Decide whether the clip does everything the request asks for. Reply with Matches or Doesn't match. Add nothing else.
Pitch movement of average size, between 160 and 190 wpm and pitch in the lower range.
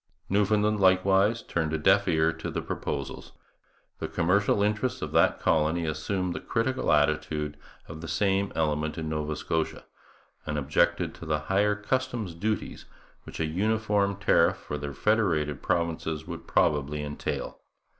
Doesn't match